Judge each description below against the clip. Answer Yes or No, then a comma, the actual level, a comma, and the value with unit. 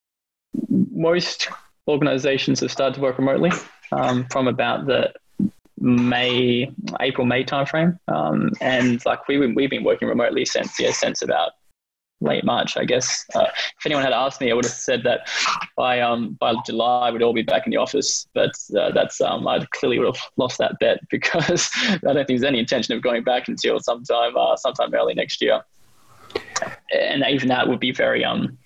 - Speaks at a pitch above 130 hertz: No, low, 125 Hz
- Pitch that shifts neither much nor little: No, narrow, 2.2 semitones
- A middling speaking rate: Yes, average, 185 wpm